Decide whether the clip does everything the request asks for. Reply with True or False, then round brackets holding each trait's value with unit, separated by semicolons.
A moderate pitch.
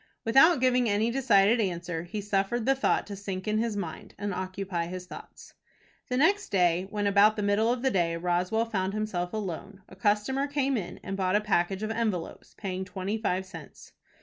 False (205 Hz)